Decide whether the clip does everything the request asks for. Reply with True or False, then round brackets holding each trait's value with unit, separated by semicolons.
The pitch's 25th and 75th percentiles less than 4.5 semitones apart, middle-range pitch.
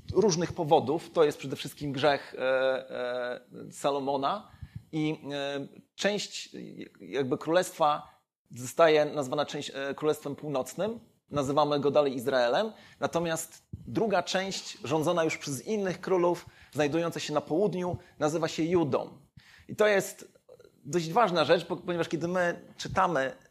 True (3.9 semitones; 155 Hz)